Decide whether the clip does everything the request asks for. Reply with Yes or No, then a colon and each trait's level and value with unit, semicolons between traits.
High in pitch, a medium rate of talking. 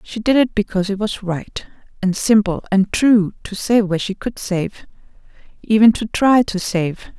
Yes: high, 205 Hz; average, 185 wpm